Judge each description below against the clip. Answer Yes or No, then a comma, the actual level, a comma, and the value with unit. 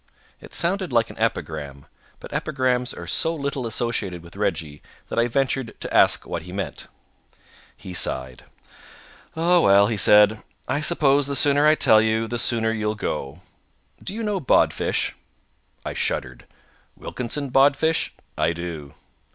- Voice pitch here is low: Yes, low, 115 Hz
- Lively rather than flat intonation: Yes, wide, 7.5 semitones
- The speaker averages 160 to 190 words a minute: No, average, 150 wpm